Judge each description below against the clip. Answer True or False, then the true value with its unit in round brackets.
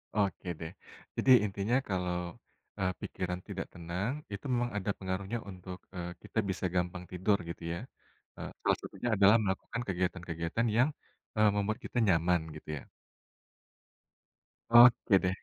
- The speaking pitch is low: True (95 Hz)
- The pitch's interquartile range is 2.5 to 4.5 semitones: True (2.8 semitones)